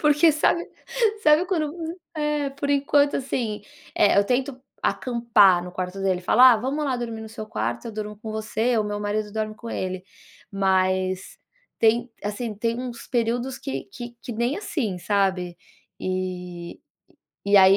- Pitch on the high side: Yes, high, 220 Hz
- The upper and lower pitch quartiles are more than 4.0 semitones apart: Yes, average, 5.1 semitones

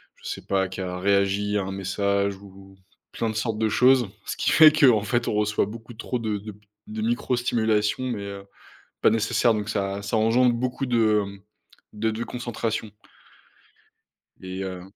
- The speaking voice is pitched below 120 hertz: Yes, low, 110 Hz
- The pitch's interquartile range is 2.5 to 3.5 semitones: Yes, average, 2.9 semitones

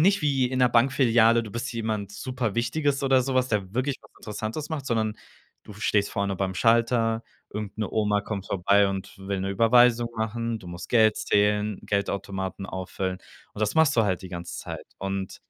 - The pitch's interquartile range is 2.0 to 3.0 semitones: No, average, 3.5 semitones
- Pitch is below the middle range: Yes, low, 110 Hz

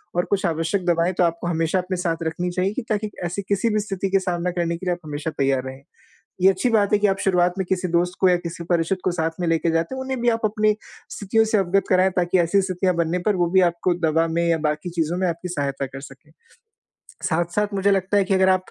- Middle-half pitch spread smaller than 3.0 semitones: Yes, narrow, 2.5 semitones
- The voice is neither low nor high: Yes, medium, 180 Hz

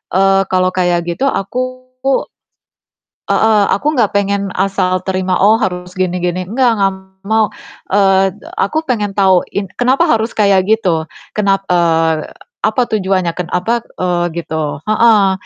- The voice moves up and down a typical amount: Yes, average, 3.2 semitones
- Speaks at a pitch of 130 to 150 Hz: No, high, 195 Hz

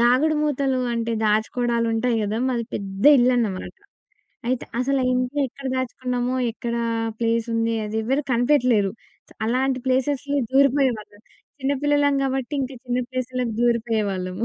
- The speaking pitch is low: No, high, 245 Hz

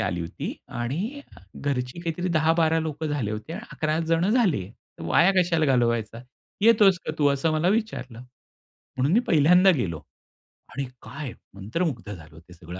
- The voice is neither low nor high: Yes, medium, 150 Hz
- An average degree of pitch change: No, wide, 6.9 semitones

